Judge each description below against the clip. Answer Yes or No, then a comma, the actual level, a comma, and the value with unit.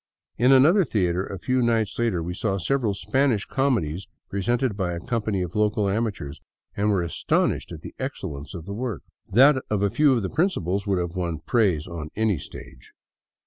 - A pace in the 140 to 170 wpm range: No, average, 185 wpm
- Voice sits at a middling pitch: No, low, 100 Hz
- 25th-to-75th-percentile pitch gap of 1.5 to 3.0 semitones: No, average, 5.2 semitones